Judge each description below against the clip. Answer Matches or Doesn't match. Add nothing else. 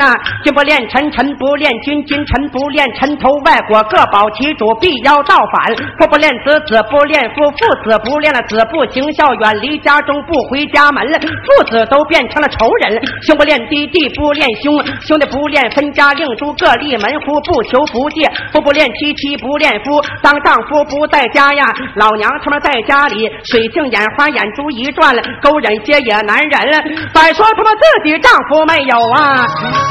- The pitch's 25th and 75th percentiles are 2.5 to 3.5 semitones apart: Matches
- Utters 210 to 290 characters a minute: Matches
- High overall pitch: Matches